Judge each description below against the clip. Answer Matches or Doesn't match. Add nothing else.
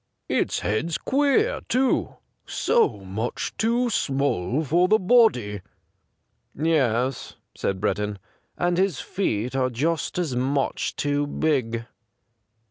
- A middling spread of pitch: Doesn't match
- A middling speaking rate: Doesn't match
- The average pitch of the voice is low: Doesn't match